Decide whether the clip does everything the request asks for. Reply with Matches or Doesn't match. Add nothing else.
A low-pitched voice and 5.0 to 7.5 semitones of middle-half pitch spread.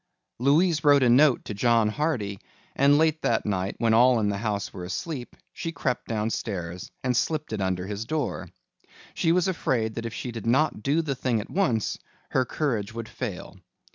Matches